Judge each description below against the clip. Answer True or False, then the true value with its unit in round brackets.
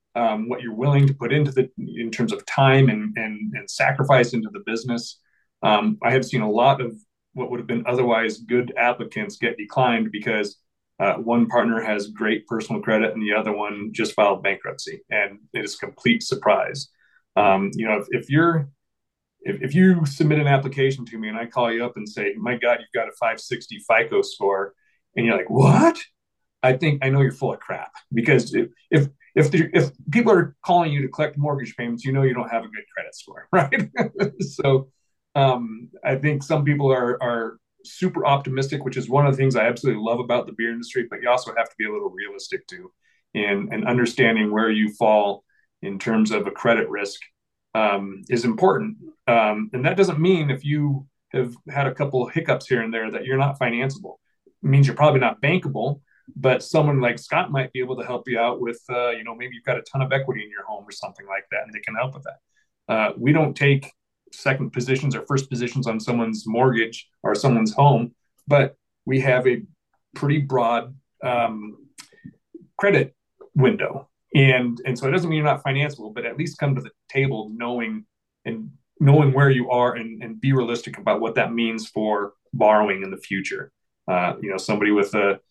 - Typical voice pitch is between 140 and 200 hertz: False (125 Hz)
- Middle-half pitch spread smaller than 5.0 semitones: True (3.5 semitones)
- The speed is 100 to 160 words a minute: False (205 wpm)